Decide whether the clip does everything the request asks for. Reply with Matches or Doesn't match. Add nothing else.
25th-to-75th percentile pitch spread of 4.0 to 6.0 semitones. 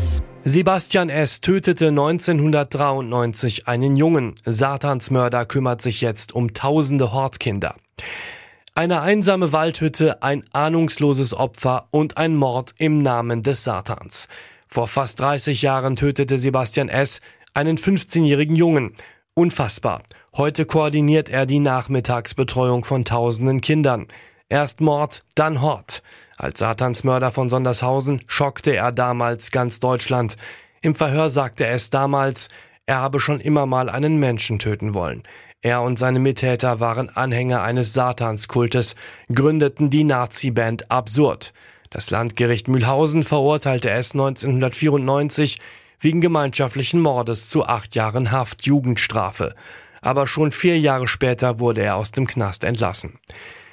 Doesn't match